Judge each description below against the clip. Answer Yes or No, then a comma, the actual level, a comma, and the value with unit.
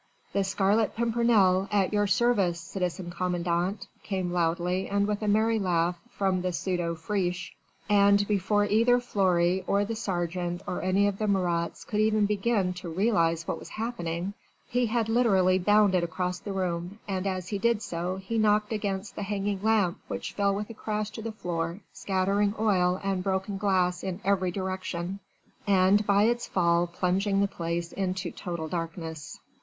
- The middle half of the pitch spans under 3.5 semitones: Yes, average, 2.7 semitones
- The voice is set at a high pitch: Yes, high, 195 Hz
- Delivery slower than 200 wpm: Yes, average, 170 wpm